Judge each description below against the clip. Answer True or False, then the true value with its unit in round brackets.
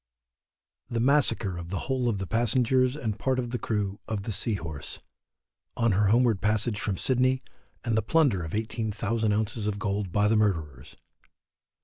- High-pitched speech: False (110 Hz)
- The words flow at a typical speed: True (170 wpm)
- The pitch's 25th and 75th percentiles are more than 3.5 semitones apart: False (3.2 semitones)